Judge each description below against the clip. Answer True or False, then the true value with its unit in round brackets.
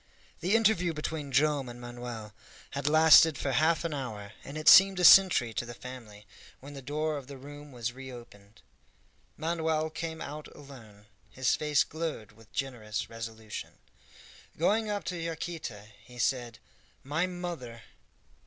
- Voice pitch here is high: False (140 Hz)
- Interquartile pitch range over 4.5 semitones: True (5.1 semitones)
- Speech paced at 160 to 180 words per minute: False (150 wpm)